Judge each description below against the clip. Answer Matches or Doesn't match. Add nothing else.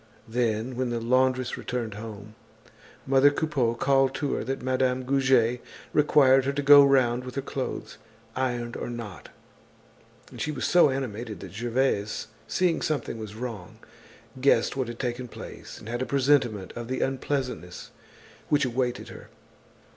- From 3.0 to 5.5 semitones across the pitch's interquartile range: Doesn't match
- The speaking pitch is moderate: Doesn't match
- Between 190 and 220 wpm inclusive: Doesn't match